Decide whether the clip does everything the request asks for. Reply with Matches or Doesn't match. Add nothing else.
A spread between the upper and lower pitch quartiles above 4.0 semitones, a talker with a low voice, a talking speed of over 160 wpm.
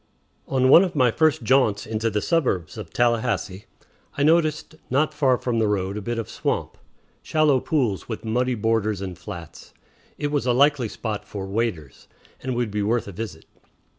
Matches